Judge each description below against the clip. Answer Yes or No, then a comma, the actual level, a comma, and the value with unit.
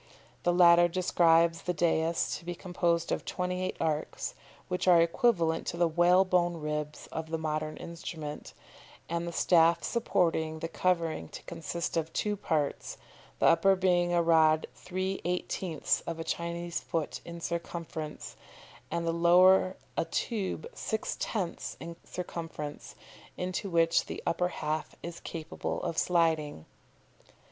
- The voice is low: No, medium, 170 Hz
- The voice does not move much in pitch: Yes, narrow, 1.7 semitones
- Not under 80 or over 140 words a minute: Yes, slow, 135 wpm